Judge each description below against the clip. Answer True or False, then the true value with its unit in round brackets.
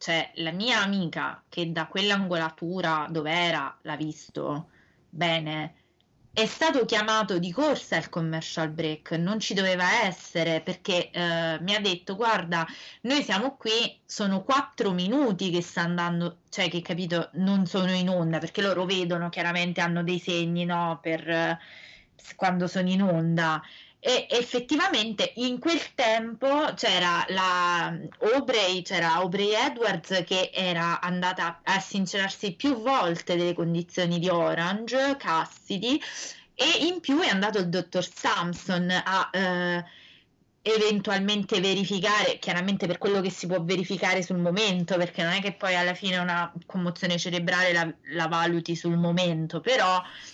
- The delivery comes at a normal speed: True (145 wpm)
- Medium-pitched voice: True (180 Hz)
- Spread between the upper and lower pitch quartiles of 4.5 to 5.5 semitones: False (2.9 semitones)